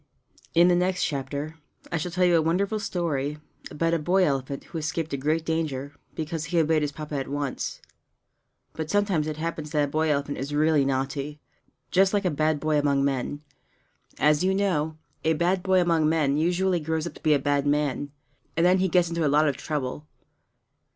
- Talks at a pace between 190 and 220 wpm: Yes, average, 200 wpm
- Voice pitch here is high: No, medium, 155 Hz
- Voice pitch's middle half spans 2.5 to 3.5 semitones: Yes, average, 3.0 semitones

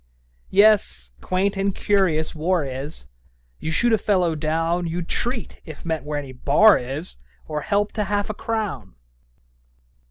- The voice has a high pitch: No, medium, 175 Hz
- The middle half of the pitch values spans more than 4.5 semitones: Yes, average, 5.1 semitones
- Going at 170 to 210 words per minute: No, average, 150 wpm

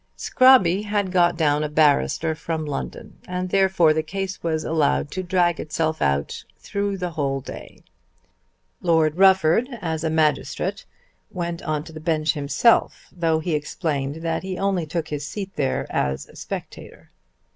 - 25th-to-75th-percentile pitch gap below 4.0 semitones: Yes, average, 3.2 semitones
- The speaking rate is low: No, average, 155 wpm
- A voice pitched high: No, medium, 165 Hz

